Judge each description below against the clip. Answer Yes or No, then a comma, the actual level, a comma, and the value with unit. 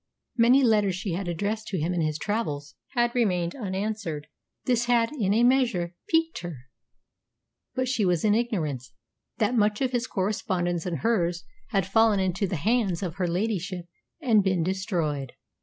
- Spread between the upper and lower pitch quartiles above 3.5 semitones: Yes, average, 4.7 semitones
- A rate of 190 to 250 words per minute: No, average, 165 wpm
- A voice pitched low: No, high, 195 Hz